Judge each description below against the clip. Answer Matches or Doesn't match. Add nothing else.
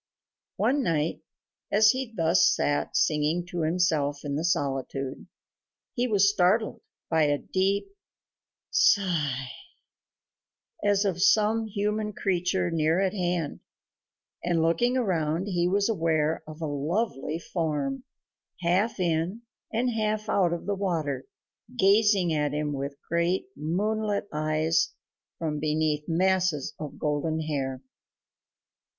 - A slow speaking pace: Matches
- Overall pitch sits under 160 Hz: Doesn't match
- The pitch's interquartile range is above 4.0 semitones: Matches